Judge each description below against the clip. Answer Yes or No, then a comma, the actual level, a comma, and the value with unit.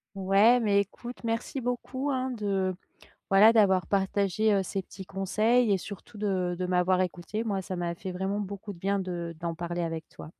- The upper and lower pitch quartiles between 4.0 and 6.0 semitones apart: No, average, 2.9 semitones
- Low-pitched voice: No, high, 195 Hz